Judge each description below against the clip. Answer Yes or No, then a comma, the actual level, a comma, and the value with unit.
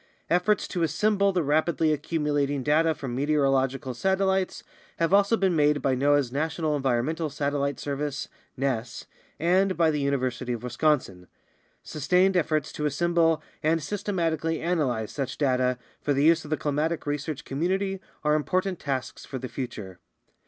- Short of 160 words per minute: Yes, average, 150 wpm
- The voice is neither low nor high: Yes, medium, 150 Hz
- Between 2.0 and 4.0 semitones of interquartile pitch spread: Yes, average, 3.7 semitones